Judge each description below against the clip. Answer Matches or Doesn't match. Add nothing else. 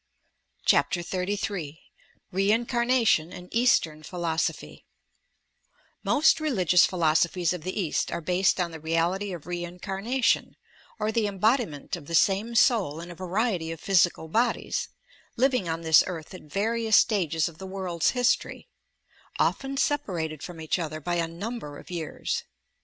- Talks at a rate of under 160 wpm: Matches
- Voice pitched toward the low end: Doesn't match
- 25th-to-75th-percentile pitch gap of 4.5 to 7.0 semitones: Matches